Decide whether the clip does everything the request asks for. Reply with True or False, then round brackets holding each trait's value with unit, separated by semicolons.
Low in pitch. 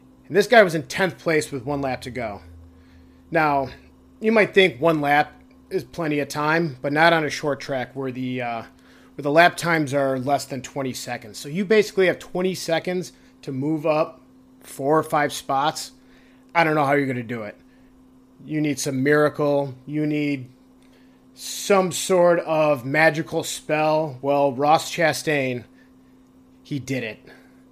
False (145 Hz)